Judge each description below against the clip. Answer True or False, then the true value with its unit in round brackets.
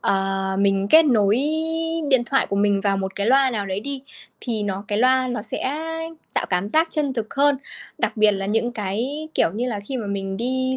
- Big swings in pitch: False (4.7 semitones)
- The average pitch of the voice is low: False (220 Hz)